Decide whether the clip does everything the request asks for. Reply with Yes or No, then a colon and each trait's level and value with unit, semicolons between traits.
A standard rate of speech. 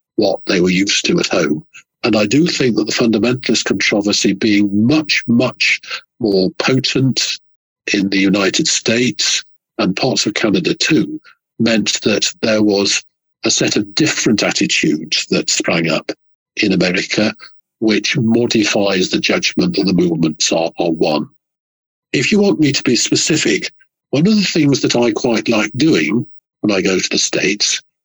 Yes: average, 160 wpm